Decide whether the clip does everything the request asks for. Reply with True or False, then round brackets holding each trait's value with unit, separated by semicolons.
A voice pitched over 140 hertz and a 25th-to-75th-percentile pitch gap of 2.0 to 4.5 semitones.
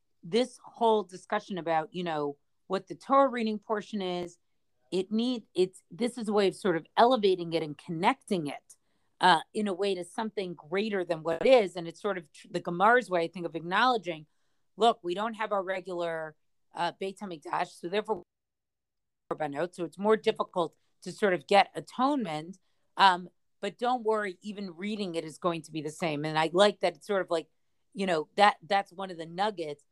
True (185 Hz; 3.9 semitones)